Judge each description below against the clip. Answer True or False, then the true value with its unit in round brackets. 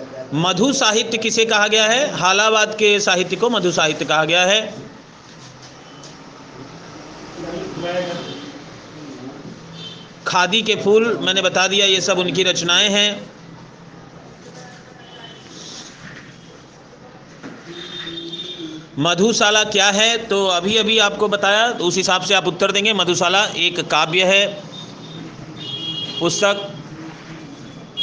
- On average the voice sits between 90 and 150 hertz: False (185 Hz)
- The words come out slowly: True (100 wpm)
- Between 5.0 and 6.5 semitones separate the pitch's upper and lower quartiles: False (3.8 semitones)